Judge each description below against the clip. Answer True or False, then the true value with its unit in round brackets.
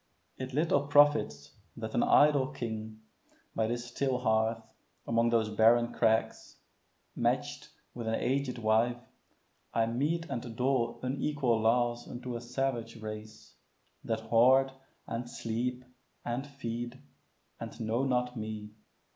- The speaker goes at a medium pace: False (125 wpm)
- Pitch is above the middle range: False (120 Hz)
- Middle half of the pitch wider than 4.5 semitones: False (2.6 semitones)